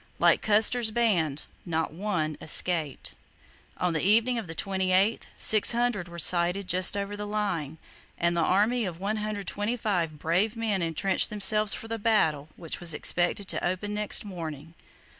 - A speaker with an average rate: Yes, average, 150 wpm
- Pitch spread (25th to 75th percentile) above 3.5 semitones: Yes, average, 3.9 semitones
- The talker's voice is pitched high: Yes, high, 195 Hz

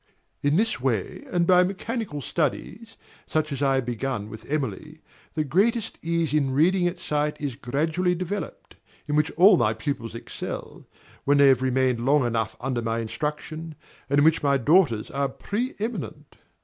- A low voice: No, medium, 150 Hz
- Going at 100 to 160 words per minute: No, average, 170 wpm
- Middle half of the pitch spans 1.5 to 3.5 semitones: No, average, 4.7 semitones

